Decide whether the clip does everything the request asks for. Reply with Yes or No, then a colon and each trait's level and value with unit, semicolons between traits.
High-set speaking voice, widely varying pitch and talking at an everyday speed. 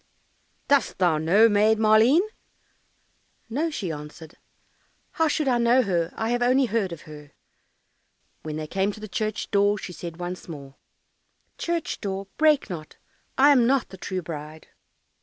Yes: high, 205 Hz; wide, 6.4 semitones; average, 160 wpm